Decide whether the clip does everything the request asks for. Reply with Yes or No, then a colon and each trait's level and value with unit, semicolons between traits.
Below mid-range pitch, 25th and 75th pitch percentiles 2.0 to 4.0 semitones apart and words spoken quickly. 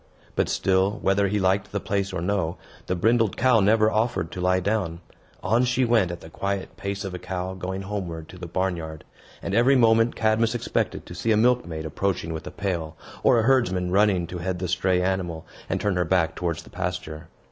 Yes: very low, 95 Hz; average, 3.3 semitones; fast, 210 wpm